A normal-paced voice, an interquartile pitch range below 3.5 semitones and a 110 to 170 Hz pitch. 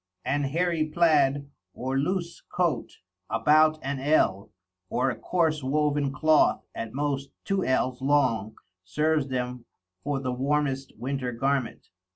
No: slow, 130 wpm; average, 2.9 semitones; medium, 140 Hz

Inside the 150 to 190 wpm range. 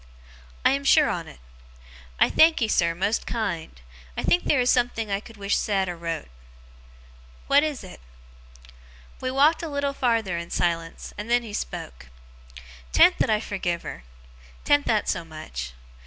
Yes: average, 160 wpm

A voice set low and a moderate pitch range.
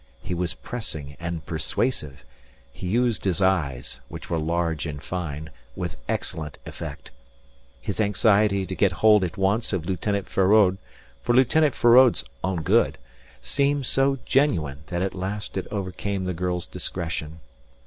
Yes: very low, 95 Hz; average, 4.4 semitones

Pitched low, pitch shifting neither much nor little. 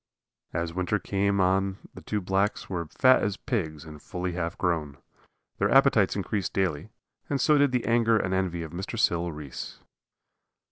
Yes: very low, 95 Hz; average, 3.8 semitones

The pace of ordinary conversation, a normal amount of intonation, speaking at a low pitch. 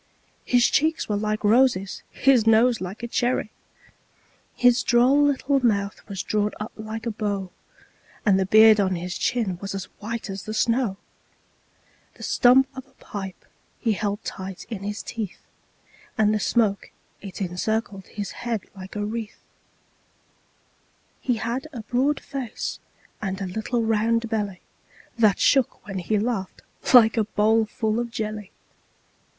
No: average, 150 wpm; average, 3.0 semitones; high, 215 Hz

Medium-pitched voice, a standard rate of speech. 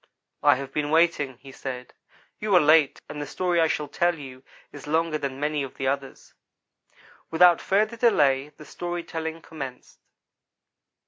Yes: medium, 150 Hz; average, 160 wpm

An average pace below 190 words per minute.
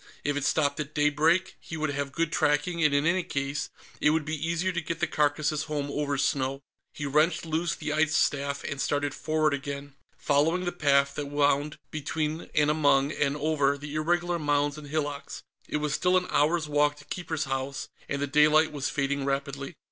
No: average, 195 wpm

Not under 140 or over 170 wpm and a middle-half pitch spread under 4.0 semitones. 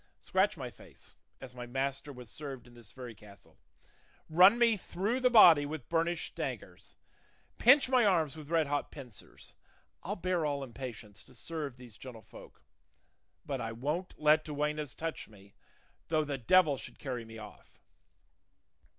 No: average, 160 wpm; average, 5.1 semitones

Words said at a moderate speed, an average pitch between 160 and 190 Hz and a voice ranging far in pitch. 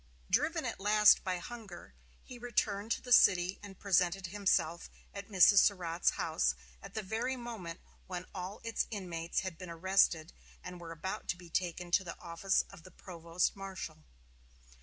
No: average, 165 wpm; medium, 185 Hz; average, 2.8 semitones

